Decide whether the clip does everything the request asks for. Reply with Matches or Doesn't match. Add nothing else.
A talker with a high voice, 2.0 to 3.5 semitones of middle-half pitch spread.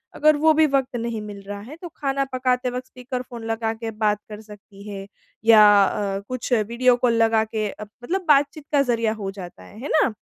Doesn't match